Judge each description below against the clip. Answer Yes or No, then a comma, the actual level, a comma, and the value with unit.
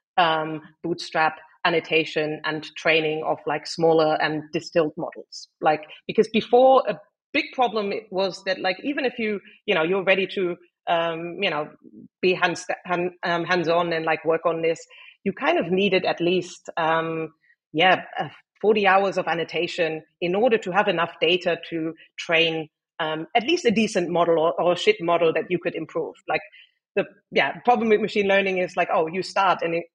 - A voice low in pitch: No, medium, 175 Hz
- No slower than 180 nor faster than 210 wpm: Yes, average, 185 wpm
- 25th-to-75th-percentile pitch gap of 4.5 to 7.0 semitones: No, average, 3.2 semitones